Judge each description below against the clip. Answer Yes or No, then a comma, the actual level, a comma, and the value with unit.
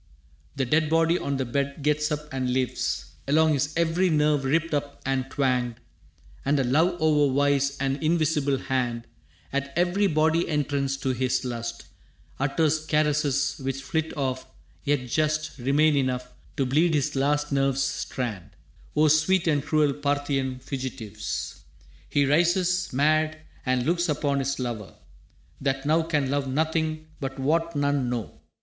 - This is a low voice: No, medium, 145 Hz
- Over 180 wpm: No, average, 150 wpm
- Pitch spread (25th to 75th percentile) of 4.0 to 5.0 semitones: No, average, 2.7 semitones